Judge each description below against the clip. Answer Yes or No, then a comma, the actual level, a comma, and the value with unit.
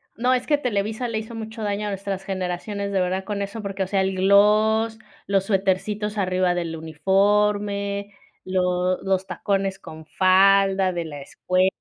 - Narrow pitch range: Yes, narrow, 1.9 semitones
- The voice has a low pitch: No, high, 195 Hz